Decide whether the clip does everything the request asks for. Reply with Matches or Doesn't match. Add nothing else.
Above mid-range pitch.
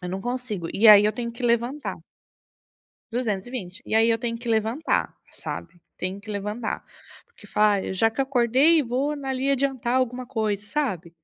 Matches